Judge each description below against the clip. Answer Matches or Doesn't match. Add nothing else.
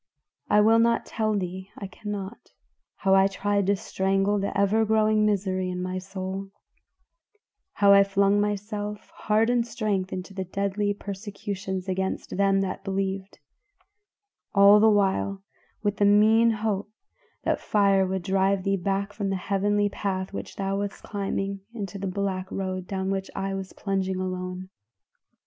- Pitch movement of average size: Doesn't match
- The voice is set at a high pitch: Matches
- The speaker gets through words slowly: Doesn't match